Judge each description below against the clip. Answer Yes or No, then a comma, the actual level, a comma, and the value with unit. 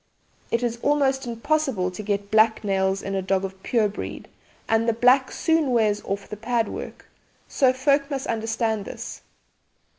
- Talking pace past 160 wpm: Yes, average, 170 wpm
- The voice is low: No, high, 225 Hz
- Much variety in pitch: No, average, 4.4 semitones